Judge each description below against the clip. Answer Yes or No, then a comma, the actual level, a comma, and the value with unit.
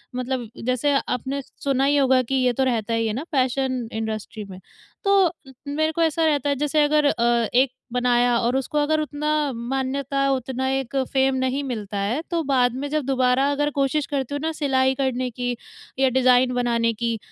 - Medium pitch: No, very high, 260 Hz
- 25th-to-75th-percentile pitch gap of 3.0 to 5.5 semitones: No, narrow, 2.6 semitones